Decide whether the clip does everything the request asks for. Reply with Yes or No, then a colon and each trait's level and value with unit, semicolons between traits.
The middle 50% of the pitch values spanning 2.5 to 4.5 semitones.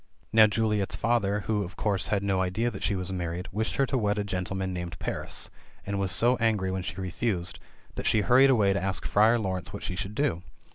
Yes: average, 3.0 semitones